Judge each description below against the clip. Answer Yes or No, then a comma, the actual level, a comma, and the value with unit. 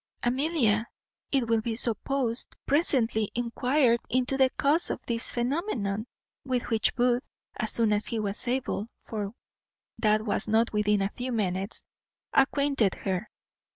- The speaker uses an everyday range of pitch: Yes, average, 3.4 semitones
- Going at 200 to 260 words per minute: No, average, 140 wpm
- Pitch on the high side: Yes, high, 235 Hz